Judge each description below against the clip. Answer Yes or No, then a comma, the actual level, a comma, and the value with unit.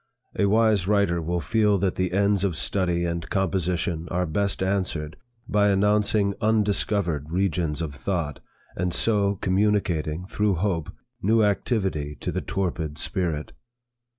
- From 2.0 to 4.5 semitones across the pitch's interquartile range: Yes, average, 3.3 semitones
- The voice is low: Yes, very low, 95 Hz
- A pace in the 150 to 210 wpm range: No, slow, 135 wpm